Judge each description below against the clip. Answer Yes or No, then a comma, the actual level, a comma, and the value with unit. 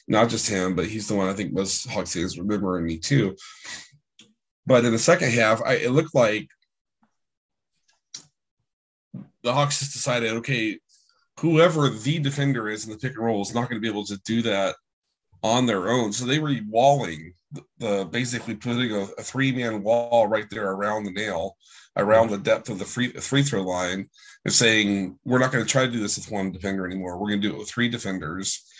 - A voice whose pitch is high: No, low, 115 Hz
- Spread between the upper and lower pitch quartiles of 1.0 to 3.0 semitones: No, average, 4.2 semitones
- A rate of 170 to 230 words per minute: Yes, average, 200 wpm